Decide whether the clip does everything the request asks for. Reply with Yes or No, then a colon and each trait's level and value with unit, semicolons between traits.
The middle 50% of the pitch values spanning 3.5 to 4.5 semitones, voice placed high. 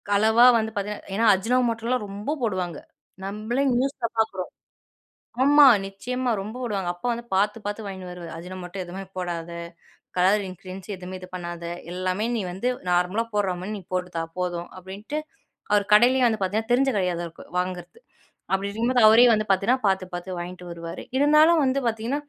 Yes: average, 4.2 semitones; high, 200 Hz